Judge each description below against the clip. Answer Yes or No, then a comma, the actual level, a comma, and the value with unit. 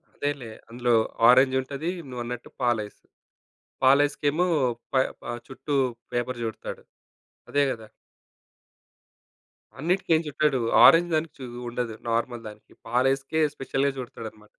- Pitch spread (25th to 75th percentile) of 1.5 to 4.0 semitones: Yes, average, 3.2 semitones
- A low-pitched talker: Yes, low, 130 Hz